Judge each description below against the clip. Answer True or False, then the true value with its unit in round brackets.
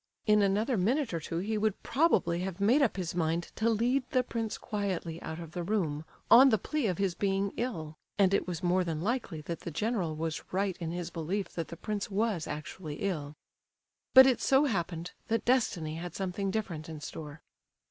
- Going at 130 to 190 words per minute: False (200 wpm)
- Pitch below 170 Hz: False (190 Hz)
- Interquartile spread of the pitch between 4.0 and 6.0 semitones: True (4.8 semitones)